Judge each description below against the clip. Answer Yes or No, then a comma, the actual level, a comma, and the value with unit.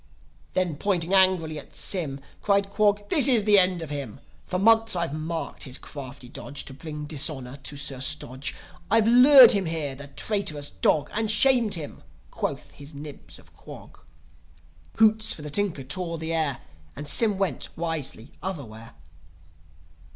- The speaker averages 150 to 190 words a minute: Yes, average, 160 wpm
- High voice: No, medium, 165 Hz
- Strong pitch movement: Yes, wide, 6.0 semitones